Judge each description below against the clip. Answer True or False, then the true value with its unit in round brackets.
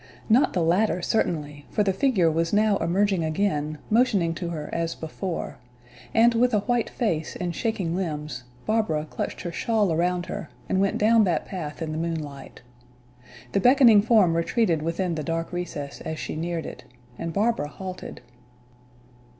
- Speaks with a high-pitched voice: False (175 Hz)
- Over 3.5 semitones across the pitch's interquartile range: True (4.6 semitones)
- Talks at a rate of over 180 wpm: False (165 wpm)